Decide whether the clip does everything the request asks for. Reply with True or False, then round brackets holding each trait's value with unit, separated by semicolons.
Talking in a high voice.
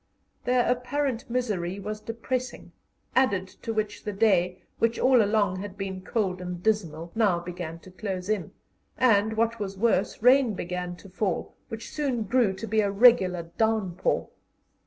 True (210 Hz)